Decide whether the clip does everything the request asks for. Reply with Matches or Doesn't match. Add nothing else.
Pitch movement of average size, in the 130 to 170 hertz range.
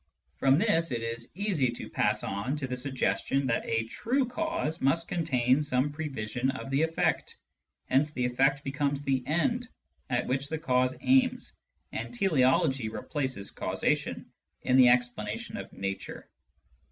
Matches